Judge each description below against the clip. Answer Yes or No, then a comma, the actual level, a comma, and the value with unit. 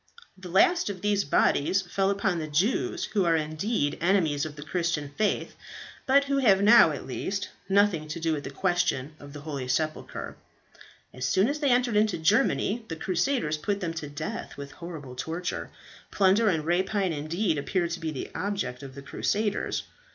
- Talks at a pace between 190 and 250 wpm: No, average, 180 wpm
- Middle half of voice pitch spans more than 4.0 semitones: Yes, average, 5.0 semitones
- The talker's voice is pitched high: No, medium, 175 Hz